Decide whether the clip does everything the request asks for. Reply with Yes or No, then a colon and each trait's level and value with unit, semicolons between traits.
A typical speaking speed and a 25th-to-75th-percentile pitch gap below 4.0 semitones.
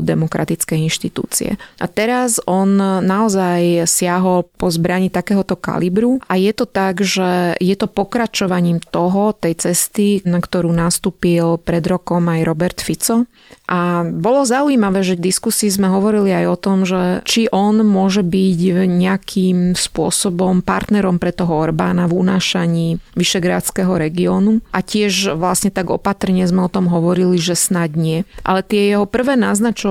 Yes: average, 145 wpm; narrow, 2.5 semitones